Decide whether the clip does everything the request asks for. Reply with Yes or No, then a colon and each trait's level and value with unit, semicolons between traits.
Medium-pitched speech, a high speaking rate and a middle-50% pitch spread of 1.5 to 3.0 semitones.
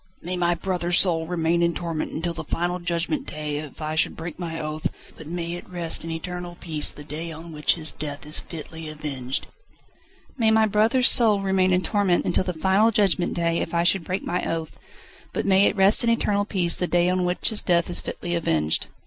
Yes: medium, 175 Hz; fast, 215 wpm; narrow, 2.4 semitones